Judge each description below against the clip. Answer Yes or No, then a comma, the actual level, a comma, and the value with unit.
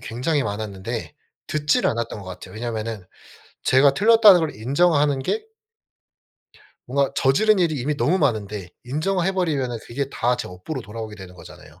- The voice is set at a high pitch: No, low, 130 Hz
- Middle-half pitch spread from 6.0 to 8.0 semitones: Yes, wide, 6.5 semitones